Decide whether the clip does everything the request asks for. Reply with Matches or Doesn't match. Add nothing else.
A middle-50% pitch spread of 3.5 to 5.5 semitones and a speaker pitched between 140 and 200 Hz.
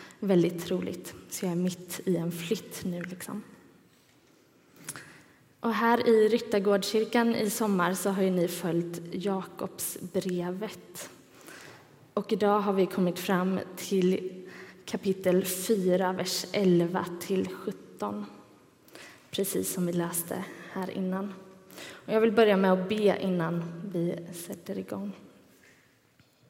Doesn't match